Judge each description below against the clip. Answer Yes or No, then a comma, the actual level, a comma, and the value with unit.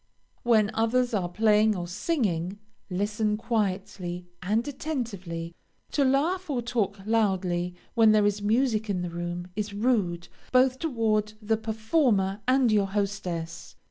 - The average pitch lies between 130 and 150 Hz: No, high, 210 Hz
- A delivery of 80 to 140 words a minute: Yes, slow, 135 wpm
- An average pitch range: Yes, average, 3.9 semitones